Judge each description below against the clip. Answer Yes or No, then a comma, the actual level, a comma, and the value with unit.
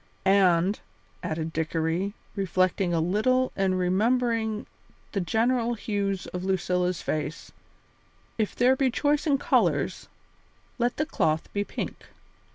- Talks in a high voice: Yes, high, 195 Hz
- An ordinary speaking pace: No, slow, 120 wpm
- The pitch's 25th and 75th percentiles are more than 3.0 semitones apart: Yes, average, 4.7 semitones